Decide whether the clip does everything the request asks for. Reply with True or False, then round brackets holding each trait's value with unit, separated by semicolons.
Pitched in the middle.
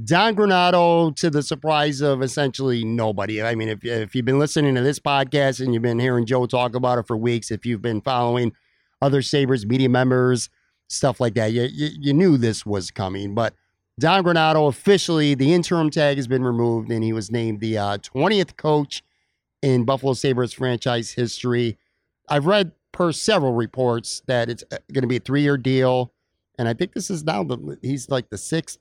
False (130 Hz)